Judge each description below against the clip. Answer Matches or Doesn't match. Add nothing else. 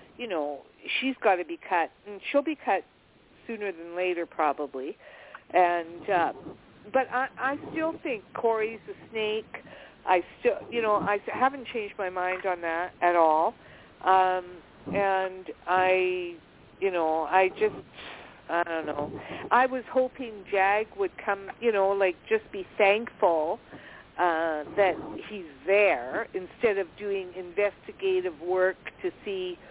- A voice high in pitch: Matches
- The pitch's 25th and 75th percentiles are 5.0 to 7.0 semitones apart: Matches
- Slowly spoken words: Doesn't match